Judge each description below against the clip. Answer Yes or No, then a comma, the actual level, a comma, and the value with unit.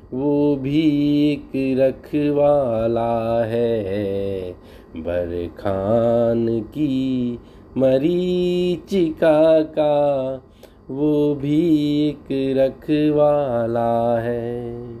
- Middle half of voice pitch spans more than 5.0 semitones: No, average, 4.2 semitones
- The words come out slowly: Yes, slow, 65 wpm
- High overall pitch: No, low, 130 Hz